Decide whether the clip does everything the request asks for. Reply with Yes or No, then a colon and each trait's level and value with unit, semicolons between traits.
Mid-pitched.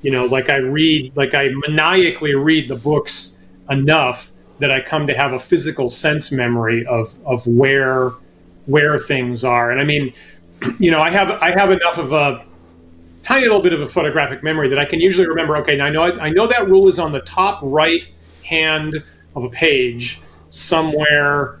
Yes: medium, 145 Hz